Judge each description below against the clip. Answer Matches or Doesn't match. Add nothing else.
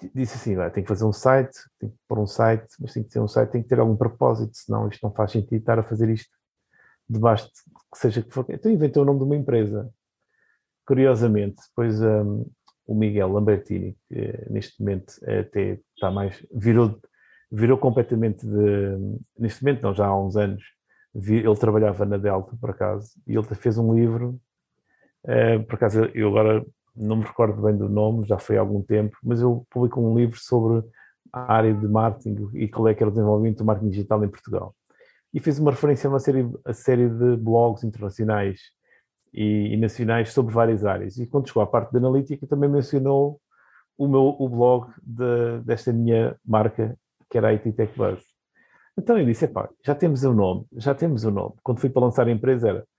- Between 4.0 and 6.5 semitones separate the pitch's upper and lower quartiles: Doesn't match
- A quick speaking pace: Matches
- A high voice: Doesn't match